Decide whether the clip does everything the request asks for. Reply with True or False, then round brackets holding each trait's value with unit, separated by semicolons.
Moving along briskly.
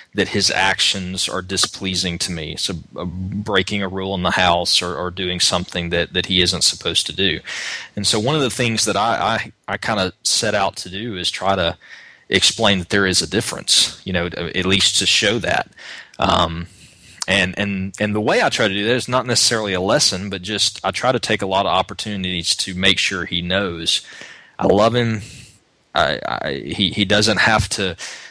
True (210 wpm)